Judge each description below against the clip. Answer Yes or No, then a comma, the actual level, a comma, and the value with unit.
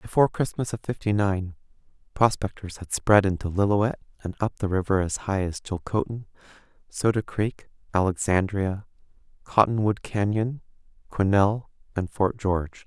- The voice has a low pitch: Yes, low, 100 Hz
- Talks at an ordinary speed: No, slow, 125 wpm